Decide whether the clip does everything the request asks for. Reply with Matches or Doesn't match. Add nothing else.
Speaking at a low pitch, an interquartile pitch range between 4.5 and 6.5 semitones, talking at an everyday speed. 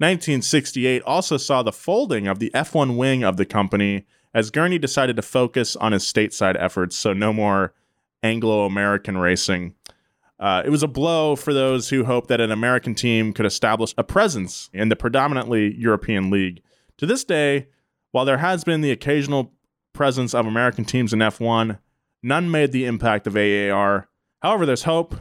Matches